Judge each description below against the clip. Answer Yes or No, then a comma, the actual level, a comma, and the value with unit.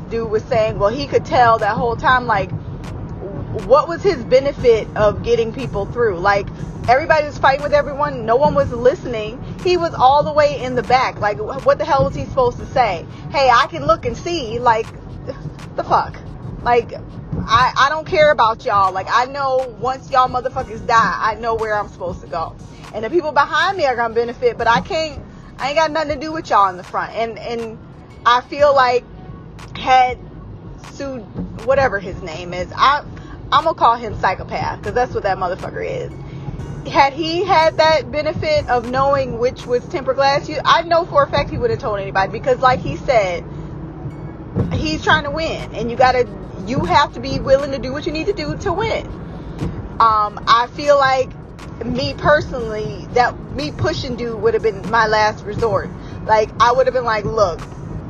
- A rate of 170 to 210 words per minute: Yes, average, 195 wpm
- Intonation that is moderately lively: No, wide, 5.8 semitones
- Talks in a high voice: Yes, very high, 255 Hz